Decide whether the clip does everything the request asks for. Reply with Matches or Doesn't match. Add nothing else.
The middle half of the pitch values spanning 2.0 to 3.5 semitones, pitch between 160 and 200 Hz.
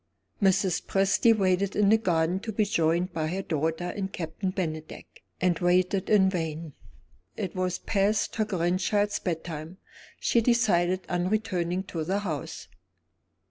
Matches